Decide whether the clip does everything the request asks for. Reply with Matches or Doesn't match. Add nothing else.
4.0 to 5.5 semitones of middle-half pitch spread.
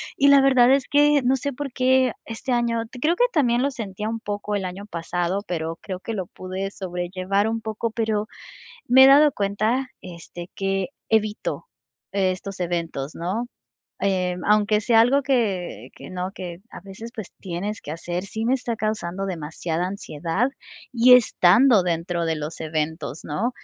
Matches